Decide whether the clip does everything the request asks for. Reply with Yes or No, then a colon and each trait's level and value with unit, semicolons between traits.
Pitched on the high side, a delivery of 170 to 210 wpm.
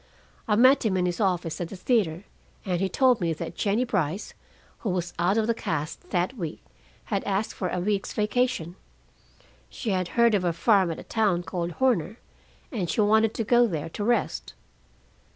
Yes: high, 195 Hz; average, 190 wpm